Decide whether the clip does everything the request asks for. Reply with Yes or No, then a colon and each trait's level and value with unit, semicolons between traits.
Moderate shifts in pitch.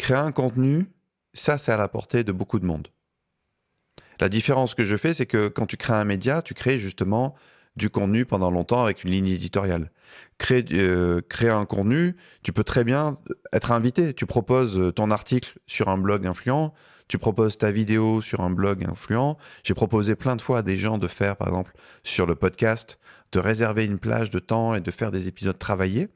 Yes: average, 4.6 semitones